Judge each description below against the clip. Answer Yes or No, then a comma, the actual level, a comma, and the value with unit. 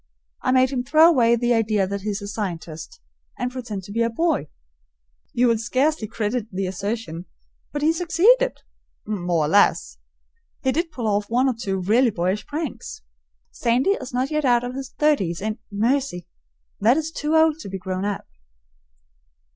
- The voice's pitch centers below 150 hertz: No, high, 235 Hz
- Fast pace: No, average, 180 wpm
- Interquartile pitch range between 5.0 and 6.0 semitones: Yes, wide, 5.4 semitones